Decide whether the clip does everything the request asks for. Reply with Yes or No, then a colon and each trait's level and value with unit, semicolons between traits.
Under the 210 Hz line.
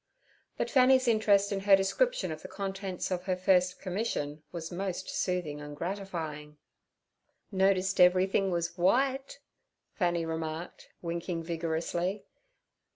Yes: medium, 185 Hz